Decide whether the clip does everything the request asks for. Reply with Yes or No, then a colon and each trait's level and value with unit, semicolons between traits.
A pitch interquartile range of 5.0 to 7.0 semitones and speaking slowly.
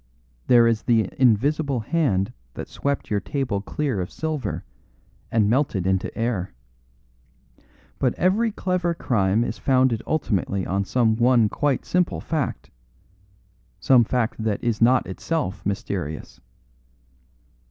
Yes: wide, 5.6 semitones; slow, 120 wpm